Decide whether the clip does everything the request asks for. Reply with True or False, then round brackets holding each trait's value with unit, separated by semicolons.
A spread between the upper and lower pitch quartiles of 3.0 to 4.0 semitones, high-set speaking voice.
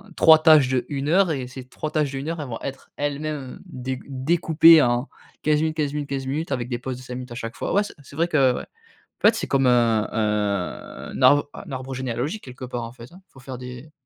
False (3.5 semitones; 135 Hz)